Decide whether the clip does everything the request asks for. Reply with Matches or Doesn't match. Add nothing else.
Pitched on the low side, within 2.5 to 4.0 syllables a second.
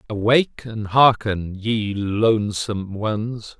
Matches